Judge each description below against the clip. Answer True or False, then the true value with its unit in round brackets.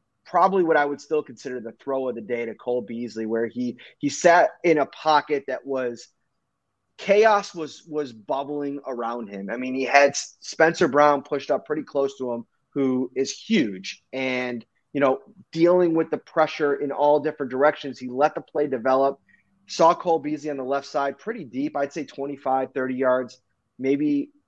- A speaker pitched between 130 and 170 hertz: True (140 Hz)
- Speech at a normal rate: True (180 wpm)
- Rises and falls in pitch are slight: False (3.3 semitones)